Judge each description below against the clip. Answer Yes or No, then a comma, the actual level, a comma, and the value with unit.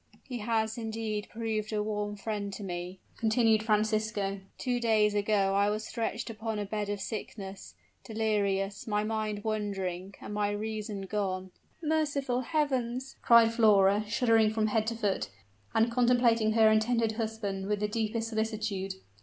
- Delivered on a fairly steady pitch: Yes, narrow, 1.7 semitones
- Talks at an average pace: Yes, average, 155 wpm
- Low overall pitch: No, high, 215 Hz